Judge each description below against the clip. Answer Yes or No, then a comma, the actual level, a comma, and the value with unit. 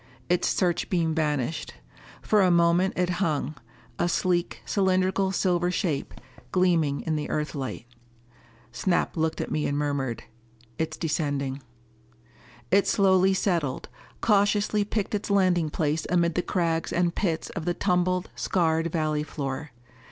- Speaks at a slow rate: Yes, slow, 130 wpm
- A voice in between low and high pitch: Yes, medium, 170 Hz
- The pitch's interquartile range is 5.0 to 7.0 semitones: No, average, 3.4 semitones